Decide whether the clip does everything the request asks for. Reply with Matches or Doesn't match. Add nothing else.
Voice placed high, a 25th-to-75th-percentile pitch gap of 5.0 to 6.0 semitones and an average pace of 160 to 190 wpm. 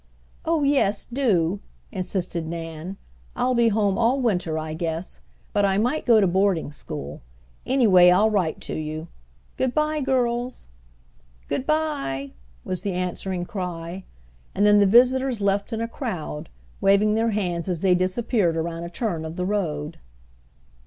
Doesn't match